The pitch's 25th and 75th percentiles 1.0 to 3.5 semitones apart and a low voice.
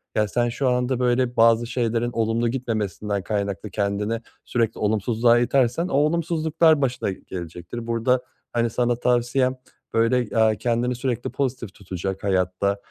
Yes: average, 2.9 semitones; low, 115 Hz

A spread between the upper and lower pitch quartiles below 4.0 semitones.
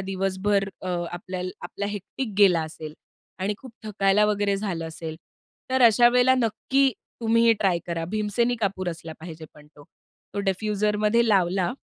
Yes: average, 3.3 semitones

